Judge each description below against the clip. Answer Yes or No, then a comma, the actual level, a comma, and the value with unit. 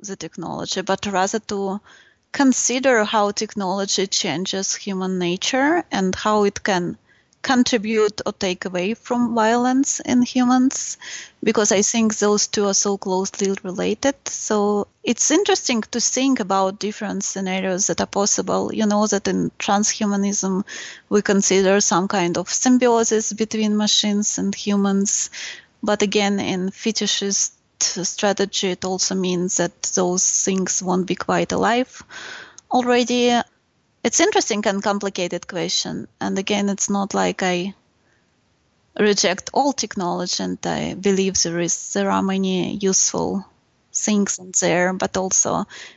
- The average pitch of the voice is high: Yes, high, 200 Hz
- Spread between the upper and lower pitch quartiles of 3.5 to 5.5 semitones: No, average, 2.8 semitones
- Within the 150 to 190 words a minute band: No, slow, 135 wpm